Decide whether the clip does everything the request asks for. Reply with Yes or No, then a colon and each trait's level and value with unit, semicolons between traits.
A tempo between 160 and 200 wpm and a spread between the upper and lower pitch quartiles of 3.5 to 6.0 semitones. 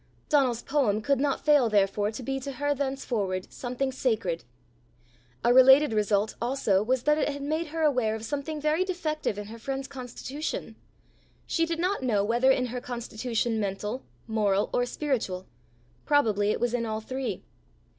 Yes: average, 165 wpm; average, 4.5 semitones